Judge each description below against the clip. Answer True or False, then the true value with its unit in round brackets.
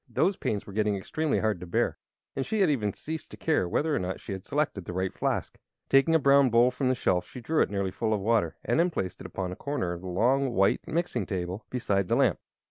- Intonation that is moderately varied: False (6.8 semitones)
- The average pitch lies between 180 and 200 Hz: False (110 Hz)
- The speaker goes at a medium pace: False (255 wpm)